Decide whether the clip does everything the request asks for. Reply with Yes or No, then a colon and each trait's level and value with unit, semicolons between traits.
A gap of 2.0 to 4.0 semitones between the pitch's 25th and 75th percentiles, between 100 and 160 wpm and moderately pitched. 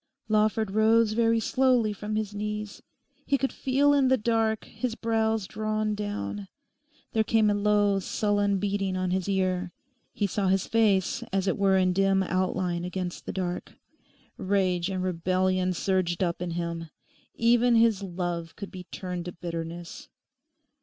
No: average, 2.8 semitones; average, 155 wpm; high, 195 Hz